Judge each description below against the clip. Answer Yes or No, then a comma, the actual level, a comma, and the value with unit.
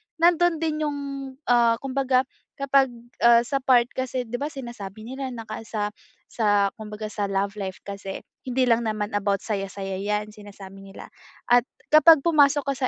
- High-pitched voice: Yes, high, 235 Hz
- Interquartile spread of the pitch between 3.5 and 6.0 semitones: Yes, average, 4.7 semitones